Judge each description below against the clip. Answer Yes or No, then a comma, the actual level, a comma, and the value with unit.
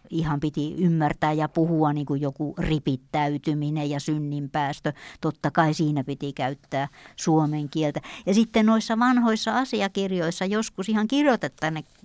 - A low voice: No, medium, 155 Hz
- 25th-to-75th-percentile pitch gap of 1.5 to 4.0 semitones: No, average, 4.5 semitones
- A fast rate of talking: No, average, 130 wpm